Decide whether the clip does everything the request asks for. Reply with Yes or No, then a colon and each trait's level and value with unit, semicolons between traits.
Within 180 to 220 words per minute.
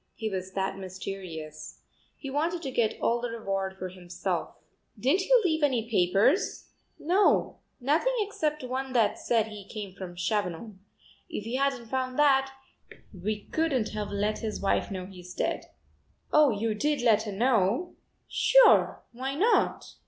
No: average, 150 wpm